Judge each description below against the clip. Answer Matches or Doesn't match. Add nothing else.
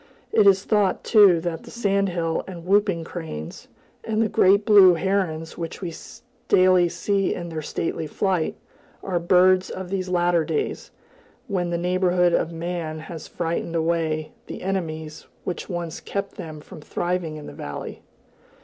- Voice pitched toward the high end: Doesn't match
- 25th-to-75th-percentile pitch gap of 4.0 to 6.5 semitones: Doesn't match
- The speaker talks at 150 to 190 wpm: Matches